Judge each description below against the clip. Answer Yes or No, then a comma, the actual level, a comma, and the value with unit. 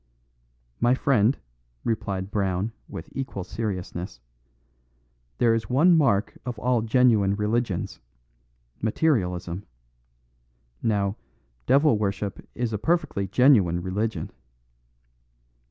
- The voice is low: Yes, low, 110 Hz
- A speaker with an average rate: No, slow, 90 wpm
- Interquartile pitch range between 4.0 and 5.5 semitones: Yes, average, 4.3 semitones